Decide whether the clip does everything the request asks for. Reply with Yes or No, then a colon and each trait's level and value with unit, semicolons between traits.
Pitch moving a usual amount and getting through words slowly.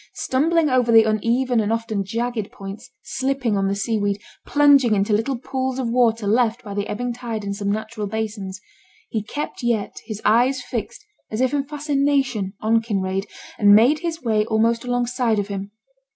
No: average, 3.4 semitones; average, 180 wpm